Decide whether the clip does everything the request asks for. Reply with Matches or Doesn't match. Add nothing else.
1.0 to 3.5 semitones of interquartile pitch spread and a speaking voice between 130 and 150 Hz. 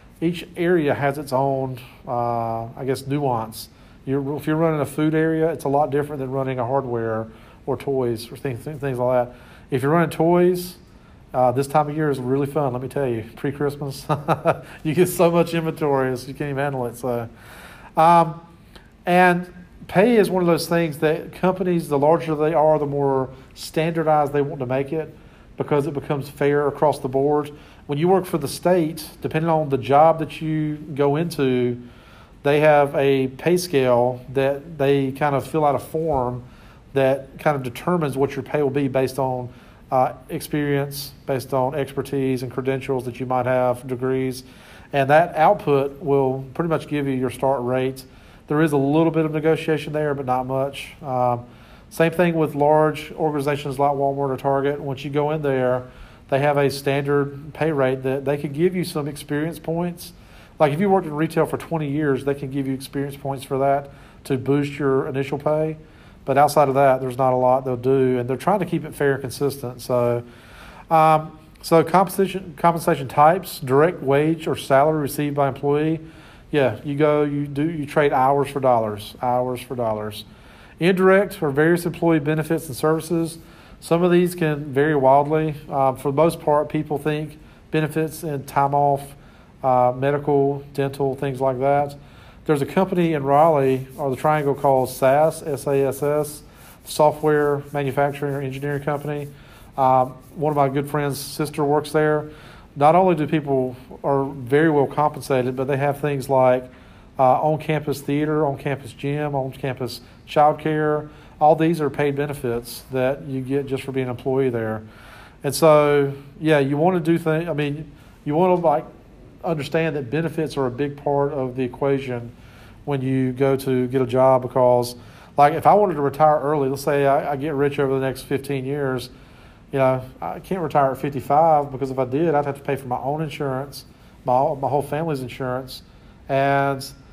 Matches